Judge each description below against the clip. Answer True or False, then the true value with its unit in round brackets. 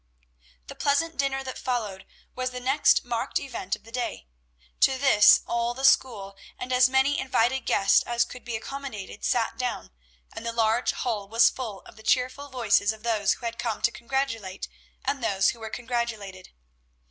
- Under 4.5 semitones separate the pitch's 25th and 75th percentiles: True (2.9 semitones)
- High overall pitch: True (235 Hz)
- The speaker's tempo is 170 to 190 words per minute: True (180 wpm)